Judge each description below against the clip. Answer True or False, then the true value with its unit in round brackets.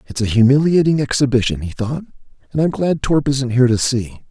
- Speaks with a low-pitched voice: True (130 Hz)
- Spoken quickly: False (195 wpm)